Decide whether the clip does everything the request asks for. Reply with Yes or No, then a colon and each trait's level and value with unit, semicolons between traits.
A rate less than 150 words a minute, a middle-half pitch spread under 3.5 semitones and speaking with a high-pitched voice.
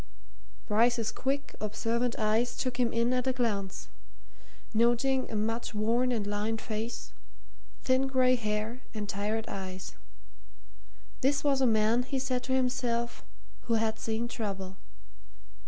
Yes: slow, 135 wpm; average, 2.8 semitones; high, 230 Hz